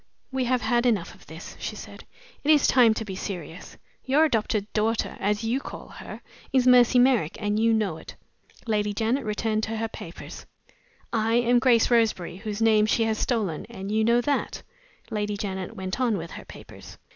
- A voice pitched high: Yes, high, 220 Hz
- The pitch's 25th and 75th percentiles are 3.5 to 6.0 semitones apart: No, average, 2.7 semitones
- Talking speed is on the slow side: No, average, 190 wpm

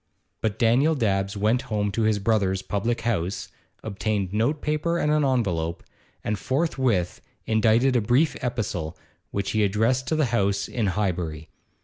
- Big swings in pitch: No, average, 4.2 semitones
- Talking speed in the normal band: Yes, average, 150 wpm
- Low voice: Yes, low, 110 Hz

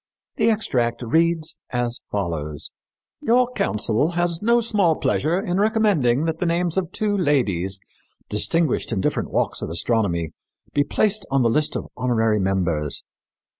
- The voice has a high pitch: No, medium, 145 Hz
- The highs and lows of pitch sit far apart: Yes, wide, 8.9 semitones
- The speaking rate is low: No, average, 145 wpm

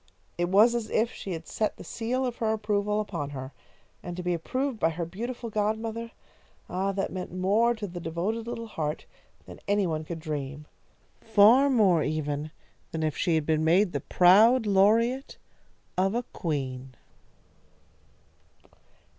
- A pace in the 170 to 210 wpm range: No, average, 160 wpm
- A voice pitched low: No, high, 195 Hz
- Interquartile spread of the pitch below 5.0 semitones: No, wide, 5.5 semitones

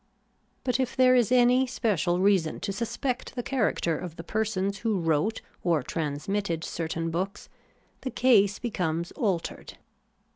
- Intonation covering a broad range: Yes, wide, 6.2 semitones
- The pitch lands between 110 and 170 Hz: No, high, 200 Hz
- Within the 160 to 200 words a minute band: No, average, 145 wpm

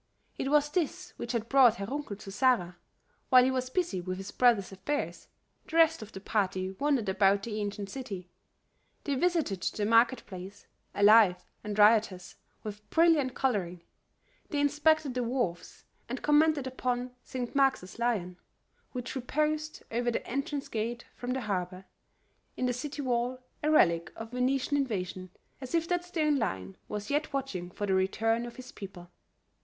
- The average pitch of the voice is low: No, high, 240 Hz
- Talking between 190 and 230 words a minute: No, average, 165 wpm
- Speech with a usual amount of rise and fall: No, wide, 5.7 semitones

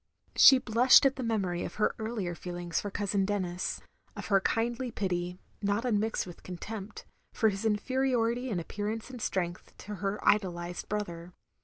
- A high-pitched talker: Yes, high, 205 Hz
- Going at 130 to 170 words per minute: Yes, average, 160 wpm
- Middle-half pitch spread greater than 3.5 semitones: Yes, average, 3.9 semitones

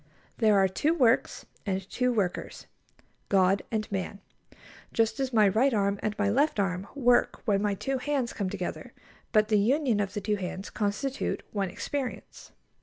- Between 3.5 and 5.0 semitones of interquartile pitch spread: Yes, average, 3.9 semitones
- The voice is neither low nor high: No, high, 210 Hz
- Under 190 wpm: Yes, average, 170 wpm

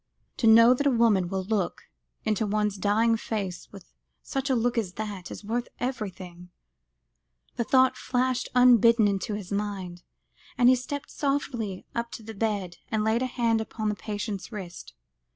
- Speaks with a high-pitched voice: Yes, high, 220 Hz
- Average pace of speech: Yes, average, 170 wpm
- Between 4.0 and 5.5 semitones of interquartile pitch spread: No, average, 3.3 semitones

